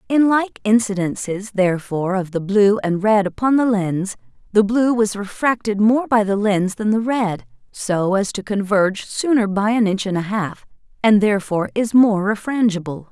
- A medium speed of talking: Yes, average, 180 wpm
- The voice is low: No, high, 205 Hz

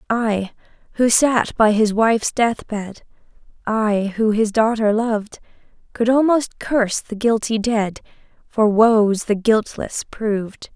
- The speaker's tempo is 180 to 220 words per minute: No, slow, 135 wpm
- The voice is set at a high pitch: Yes, high, 220 Hz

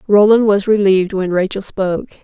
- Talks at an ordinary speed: Yes, average, 160 wpm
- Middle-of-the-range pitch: No, high, 200 Hz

